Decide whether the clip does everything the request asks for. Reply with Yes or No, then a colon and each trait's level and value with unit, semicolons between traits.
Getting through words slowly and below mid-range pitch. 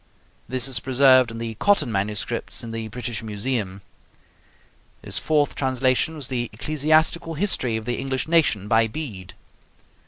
No: average, 145 wpm; low, 125 Hz